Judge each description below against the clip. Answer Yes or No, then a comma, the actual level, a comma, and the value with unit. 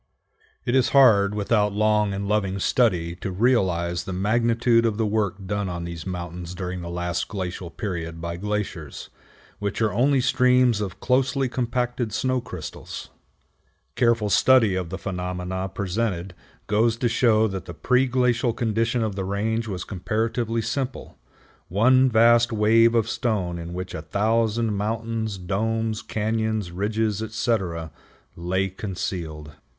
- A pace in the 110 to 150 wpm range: Yes, average, 145 wpm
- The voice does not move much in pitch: No, average, 4.0 semitones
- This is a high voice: No, low, 105 Hz